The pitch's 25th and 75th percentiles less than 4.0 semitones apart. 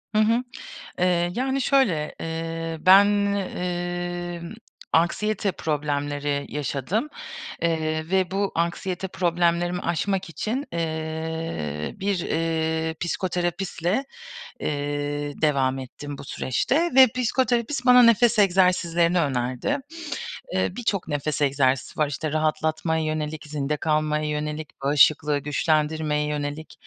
Yes: average, 3.6 semitones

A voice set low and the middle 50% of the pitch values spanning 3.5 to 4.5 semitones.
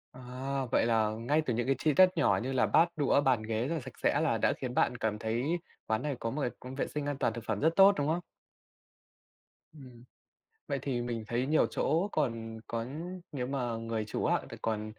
Yes: low, 125 Hz; average, 4.0 semitones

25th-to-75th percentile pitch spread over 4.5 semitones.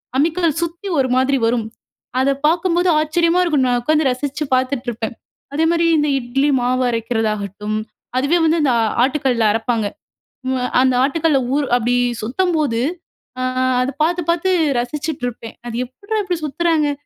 Yes: average, 5.0 semitones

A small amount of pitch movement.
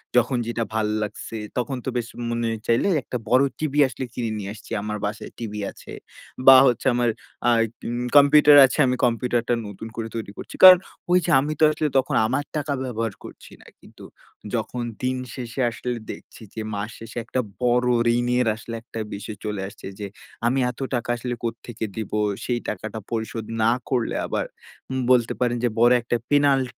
Yes: narrow, 2.3 semitones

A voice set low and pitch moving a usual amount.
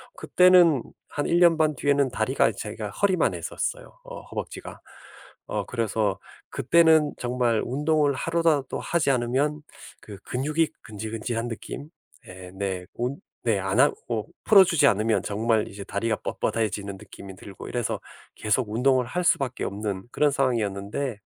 No: low, 125 Hz; wide, 5.8 semitones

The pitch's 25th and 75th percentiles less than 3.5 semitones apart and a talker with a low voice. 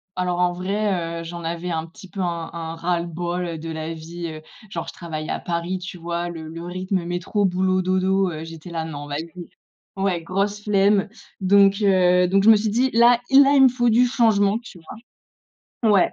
No: average, 2.9 semitones; medium, 180 Hz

